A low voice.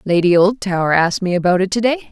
No: high, 190 Hz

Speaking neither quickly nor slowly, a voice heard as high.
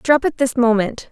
No: fast, 215 wpm; very high, 250 Hz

